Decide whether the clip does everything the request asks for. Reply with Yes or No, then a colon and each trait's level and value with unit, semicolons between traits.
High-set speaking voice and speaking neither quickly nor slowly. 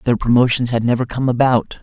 No: low, 120 Hz; average, 195 wpm